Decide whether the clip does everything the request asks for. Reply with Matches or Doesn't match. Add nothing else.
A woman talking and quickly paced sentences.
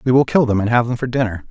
Doesn't match